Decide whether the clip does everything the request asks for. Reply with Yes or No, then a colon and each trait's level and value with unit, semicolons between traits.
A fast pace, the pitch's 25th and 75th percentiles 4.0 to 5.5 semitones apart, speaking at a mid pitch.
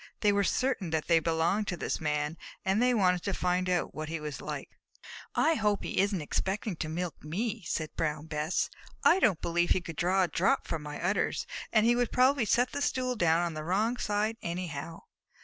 Yes: fast, 210 wpm; average, 4.9 semitones; medium, 180 Hz